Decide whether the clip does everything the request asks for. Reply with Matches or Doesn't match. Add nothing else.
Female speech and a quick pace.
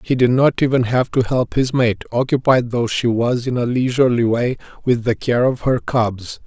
Doesn't match